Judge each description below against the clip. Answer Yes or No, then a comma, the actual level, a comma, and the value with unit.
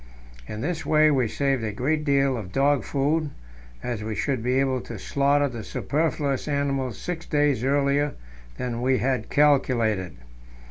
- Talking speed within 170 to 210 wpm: No, average, 155 wpm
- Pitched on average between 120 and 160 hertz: Yes, low, 135 Hz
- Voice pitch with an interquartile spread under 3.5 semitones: Yes, average, 3.1 semitones